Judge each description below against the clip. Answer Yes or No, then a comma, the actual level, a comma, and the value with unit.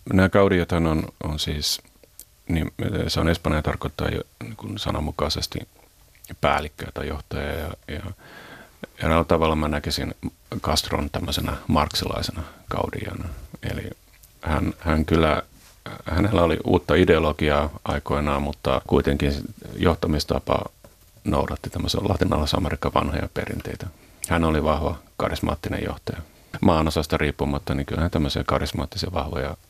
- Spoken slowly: No, average, 115 wpm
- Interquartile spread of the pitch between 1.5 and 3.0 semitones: No, average, 3.8 semitones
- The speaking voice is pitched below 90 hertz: Yes, very low, 80 Hz